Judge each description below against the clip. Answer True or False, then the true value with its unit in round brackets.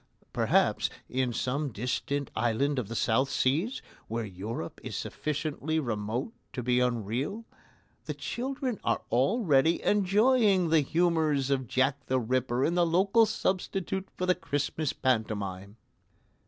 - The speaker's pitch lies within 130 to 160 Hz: True (140 Hz)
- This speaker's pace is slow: True (130 wpm)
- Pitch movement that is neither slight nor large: False (6.7 semitones)